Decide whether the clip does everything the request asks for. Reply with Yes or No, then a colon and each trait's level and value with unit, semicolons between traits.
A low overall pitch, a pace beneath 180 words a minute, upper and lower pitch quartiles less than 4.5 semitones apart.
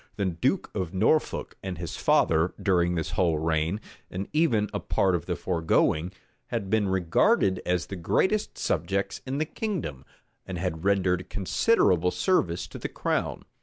Yes: very low, 95 Hz; average, 160 wpm; average, 3.6 semitones